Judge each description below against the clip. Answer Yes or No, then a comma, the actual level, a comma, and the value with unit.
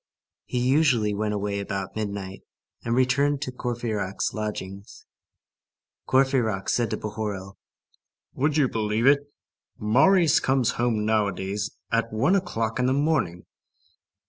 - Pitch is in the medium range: No, low, 115 Hz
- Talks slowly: Yes, slow, 120 wpm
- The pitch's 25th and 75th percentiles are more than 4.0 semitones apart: Yes, average, 4.4 semitones